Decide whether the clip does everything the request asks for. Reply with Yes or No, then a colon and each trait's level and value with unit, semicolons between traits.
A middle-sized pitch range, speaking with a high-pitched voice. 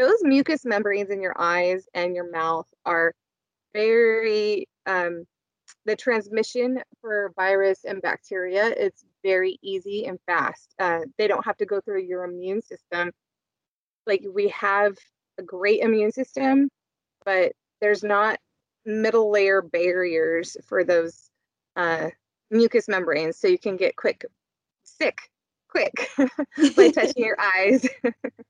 No: wide, 6.2 semitones; high, 205 Hz